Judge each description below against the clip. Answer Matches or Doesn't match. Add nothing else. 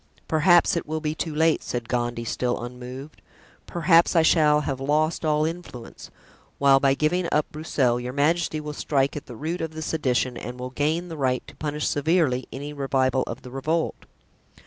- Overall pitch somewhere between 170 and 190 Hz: Doesn't match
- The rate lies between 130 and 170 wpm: Doesn't match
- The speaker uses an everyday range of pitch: Matches